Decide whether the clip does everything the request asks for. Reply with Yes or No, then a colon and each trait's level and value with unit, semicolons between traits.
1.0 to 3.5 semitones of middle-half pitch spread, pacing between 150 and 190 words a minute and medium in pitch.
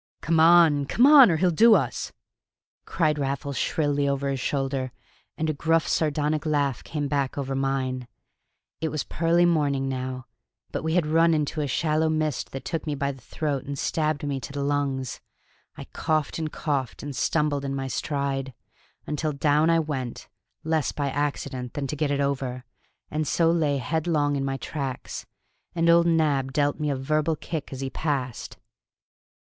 Yes: narrow, 2.5 semitones; average, 175 wpm; medium, 145 Hz